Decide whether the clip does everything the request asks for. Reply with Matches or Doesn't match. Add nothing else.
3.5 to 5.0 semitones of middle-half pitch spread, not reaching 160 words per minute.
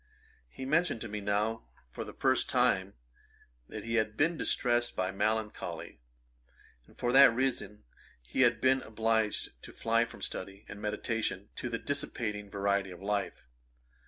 Doesn't match